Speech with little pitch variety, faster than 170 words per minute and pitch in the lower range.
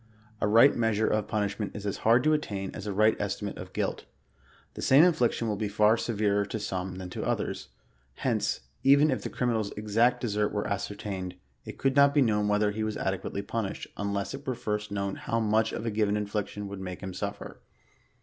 Yes: narrow, 2.2 semitones; average, 200 wpm; low, 105 Hz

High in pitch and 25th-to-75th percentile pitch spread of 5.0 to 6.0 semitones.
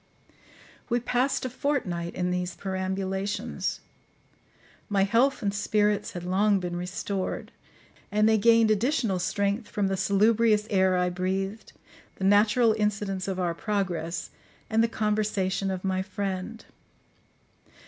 No: high, 200 Hz; narrow, 2.4 semitones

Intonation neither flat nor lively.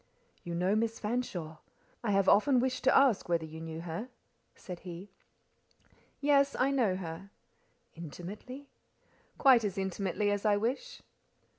No: wide, 6.3 semitones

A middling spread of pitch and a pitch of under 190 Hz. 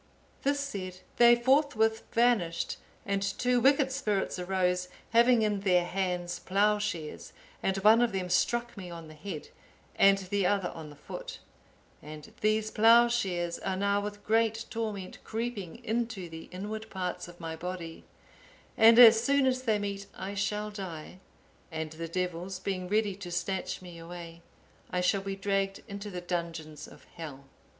No: average, 3.8 semitones; high, 195 Hz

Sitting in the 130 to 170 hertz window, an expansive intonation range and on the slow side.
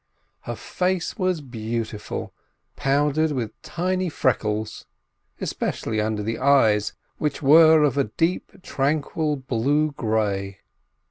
Yes: medium, 140 Hz; wide, 6.0 semitones; slow, 110 wpm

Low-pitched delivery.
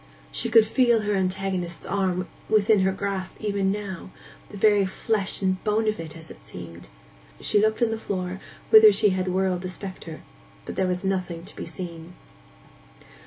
No: high, 190 Hz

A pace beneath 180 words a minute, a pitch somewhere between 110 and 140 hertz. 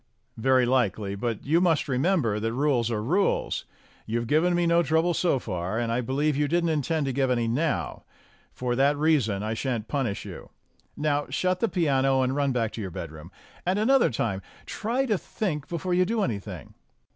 No: average, 195 wpm; low, 135 Hz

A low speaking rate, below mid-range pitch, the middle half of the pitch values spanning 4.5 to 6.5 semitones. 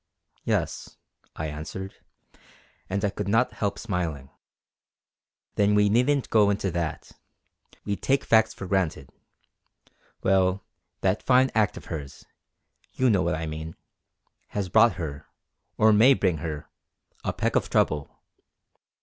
Yes: slow, 130 wpm; very low, 95 Hz; average, 4.9 semitones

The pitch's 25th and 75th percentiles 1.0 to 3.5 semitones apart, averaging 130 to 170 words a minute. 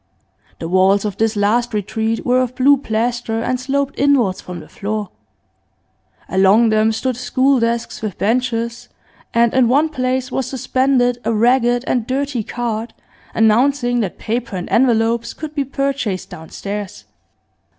Yes: average, 2.9 semitones; average, 145 wpm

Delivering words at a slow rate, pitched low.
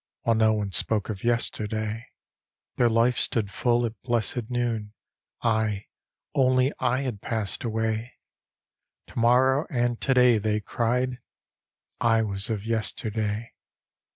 Yes: slow, 125 wpm; low, 115 Hz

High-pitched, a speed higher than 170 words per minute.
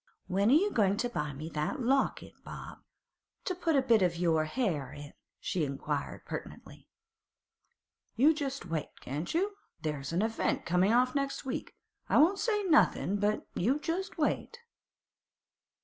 No: high, 225 Hz; average, 155 wpm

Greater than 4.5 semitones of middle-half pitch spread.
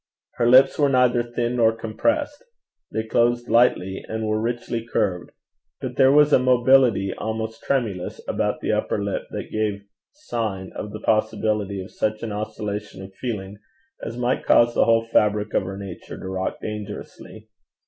No: average, 2.7 semitones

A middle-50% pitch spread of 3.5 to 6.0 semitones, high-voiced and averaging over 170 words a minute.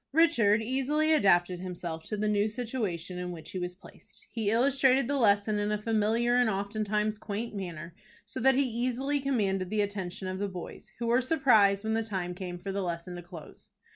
Yes: average, 4.3 semitones; high, 210 Hz; average, 200 wpm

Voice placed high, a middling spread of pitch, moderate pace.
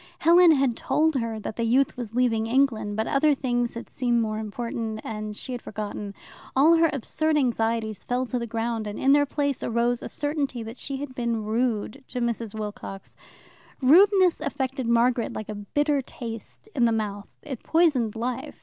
Yes: high, 240 Hz; average, 3.7 semitones; average, 185 wpm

